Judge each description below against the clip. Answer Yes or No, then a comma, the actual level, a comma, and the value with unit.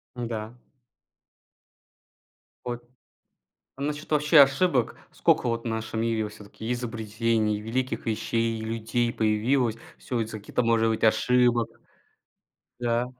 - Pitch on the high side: No, low, 115 Hz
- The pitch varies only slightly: Yes, narrow, 1.8 semitones